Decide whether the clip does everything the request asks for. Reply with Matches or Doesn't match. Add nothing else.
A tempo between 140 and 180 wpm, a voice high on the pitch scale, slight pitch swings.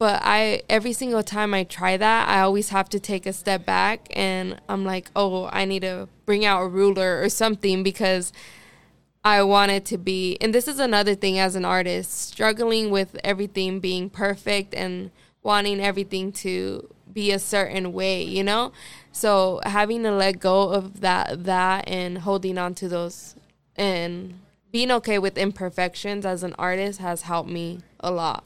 Matches